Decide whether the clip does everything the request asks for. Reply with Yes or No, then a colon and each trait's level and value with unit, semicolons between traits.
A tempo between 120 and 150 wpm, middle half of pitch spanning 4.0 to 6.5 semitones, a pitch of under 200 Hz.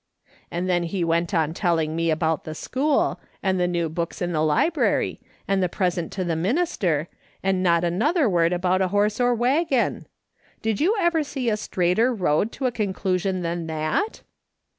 No: average, 180 wpm; average, 5.1 semitones; medium, 185 Hz